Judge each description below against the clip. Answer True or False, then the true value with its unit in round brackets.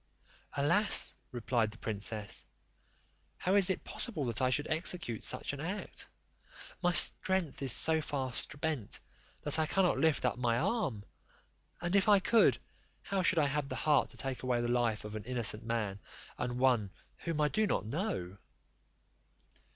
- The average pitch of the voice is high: False (140 Hz)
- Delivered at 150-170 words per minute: True (165 wpm)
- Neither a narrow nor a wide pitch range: False (6.6 semitones)